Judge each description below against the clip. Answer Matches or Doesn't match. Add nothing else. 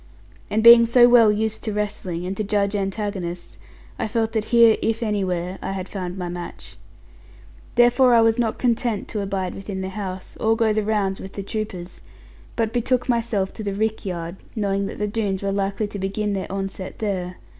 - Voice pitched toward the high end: Matches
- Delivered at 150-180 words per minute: Doesn't match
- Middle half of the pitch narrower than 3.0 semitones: Matches